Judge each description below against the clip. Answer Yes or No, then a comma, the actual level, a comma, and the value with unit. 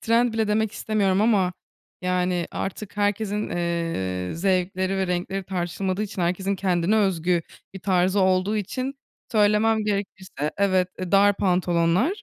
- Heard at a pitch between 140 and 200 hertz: Yes, high, 190 Hz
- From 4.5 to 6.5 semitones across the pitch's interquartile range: No, narrow, 2.6 semitones